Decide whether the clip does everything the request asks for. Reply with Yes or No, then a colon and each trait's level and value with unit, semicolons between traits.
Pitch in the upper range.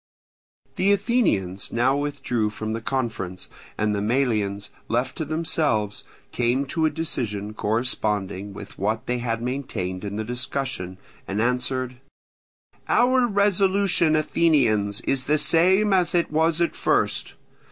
No: low, 125 Hz